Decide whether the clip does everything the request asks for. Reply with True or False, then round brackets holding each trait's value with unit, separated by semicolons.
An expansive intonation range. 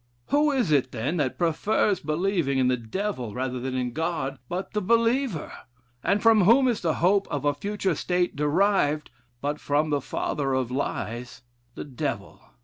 True (7.0 semitones)